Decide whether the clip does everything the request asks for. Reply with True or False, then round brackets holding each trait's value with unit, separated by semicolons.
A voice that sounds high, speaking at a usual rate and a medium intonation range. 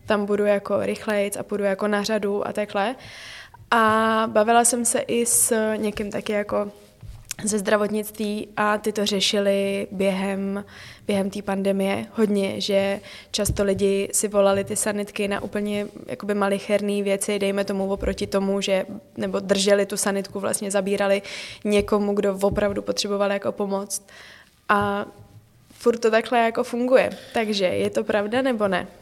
False (205 Hz; 150 wpm; 1.2 semitones)